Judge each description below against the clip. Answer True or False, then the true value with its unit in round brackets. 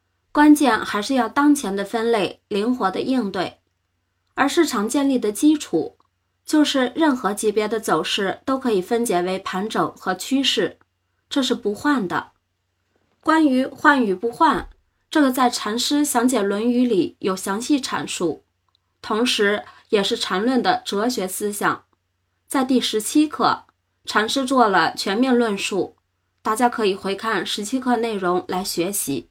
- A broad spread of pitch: False (4.8 semitones)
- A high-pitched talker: True (235 Hz)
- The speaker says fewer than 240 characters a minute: True (220 characters per minute)